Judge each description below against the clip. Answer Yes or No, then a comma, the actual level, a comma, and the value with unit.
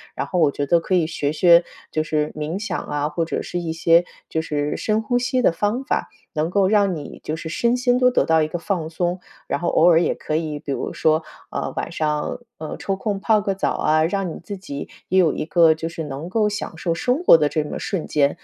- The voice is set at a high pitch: No, medium, 165 Hz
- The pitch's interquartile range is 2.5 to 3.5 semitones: No, average, 4.0 semitones